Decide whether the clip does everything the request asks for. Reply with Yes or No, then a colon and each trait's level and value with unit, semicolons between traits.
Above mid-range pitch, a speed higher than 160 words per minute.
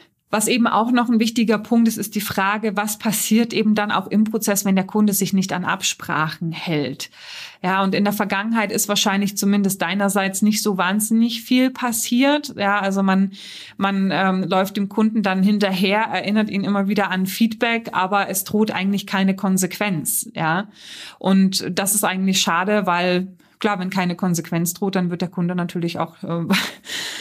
Yes: high, 200 Hz; average, 180 wpm